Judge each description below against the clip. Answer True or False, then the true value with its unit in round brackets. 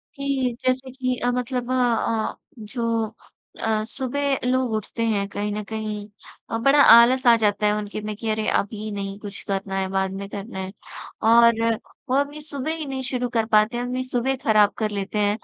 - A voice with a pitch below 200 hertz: False (230 Hz)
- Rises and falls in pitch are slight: False (3.5 semitones)